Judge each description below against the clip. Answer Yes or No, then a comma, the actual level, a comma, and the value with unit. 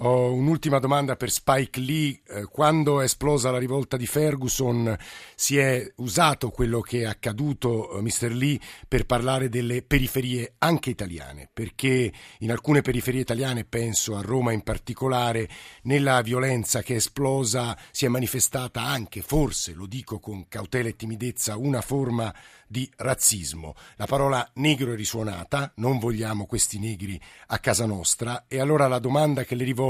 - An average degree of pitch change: Yes, average, 3.0 semitones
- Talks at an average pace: Yes, average, 160 wpm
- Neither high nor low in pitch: No, low, 125 Hz